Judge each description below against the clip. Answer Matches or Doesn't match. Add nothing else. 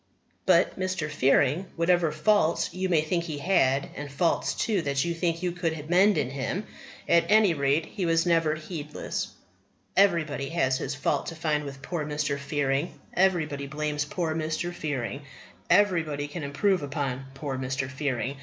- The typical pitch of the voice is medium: Matches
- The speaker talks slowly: Doesn't match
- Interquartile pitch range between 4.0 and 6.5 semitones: Doesn't match